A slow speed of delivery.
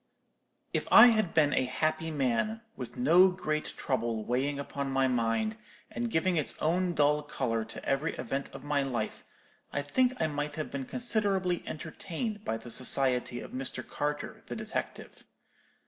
No: average, 160 wpm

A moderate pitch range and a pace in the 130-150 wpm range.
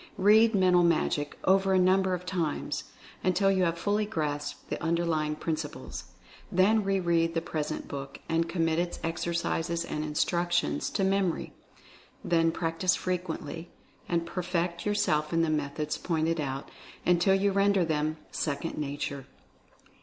Yes: average, 3.0 semitones; average, 145 wpm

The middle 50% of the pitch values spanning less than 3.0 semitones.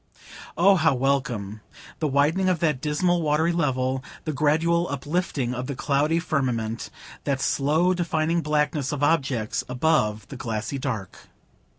No: average, 4.0 semitones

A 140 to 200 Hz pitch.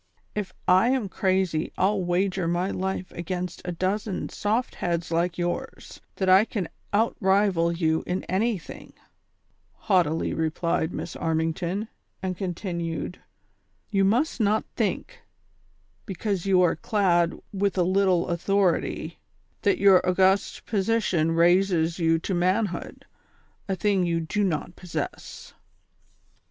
Yes: medium, 185 Hz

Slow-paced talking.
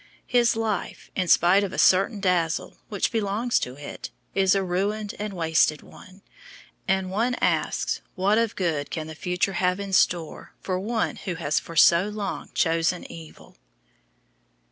No: average, 160 wpm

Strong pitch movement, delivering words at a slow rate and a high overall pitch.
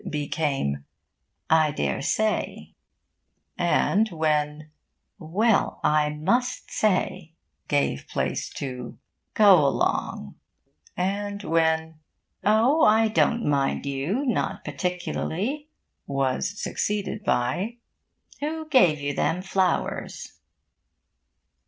No: wide, 6.2 semitones; slow, 85 wpm; medium, 175 Hz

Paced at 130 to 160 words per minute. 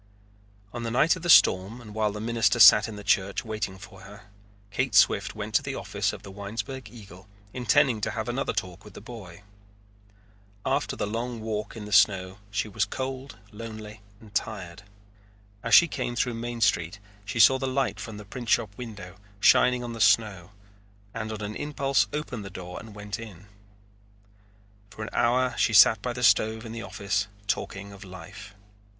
No: average, 185 wpm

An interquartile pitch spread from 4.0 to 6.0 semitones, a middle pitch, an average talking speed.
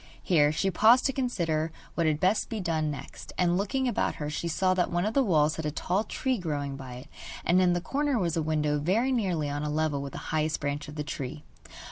No: average, 4.5 semitones; medium, 165 Hz; fast, 240 wpm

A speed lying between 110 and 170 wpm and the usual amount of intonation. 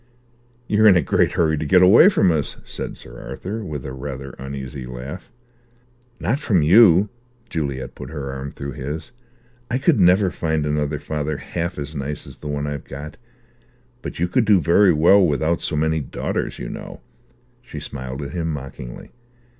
No: average, 180 wpm; average, 4.3 semitones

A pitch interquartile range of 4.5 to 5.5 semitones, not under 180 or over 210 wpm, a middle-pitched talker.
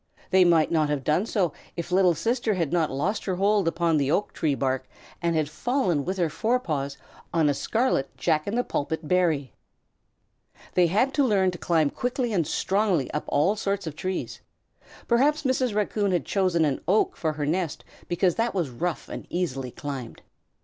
Yes: average, 5.0 semitones; average, 185 wpm; medium, 175 Hz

